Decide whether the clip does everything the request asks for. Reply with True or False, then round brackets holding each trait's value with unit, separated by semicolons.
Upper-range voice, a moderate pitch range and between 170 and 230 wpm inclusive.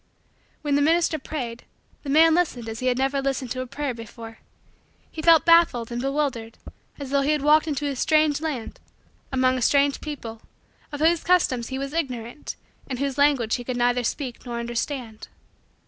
True (275 Hz; 3.7 semitones; 180 wpm)